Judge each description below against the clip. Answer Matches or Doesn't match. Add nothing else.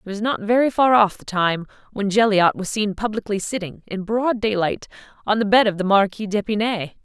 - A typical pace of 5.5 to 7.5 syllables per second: Matches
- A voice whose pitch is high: Matches